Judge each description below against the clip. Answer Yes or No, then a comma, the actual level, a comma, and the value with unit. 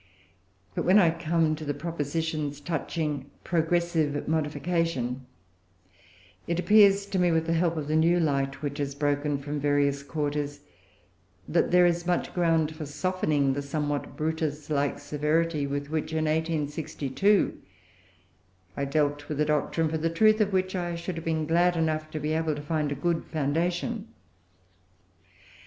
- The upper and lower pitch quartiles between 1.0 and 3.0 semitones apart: Yes, narrow, 2.6 semitones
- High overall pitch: No, medium, 155 Hz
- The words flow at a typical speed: Yes, average, 155 wpm